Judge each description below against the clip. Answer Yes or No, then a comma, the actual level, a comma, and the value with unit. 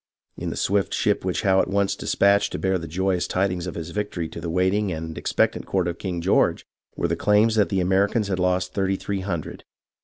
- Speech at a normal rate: No, fast, 215 wpm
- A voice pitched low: Yes, very low, 95 Hz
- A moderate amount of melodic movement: No, narrow, 2.0 semitones